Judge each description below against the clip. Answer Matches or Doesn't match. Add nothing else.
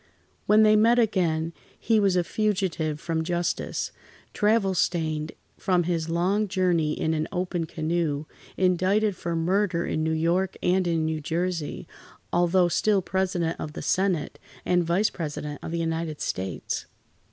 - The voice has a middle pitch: Matches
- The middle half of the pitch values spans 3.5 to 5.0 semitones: Doesn't match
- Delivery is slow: Doesn't match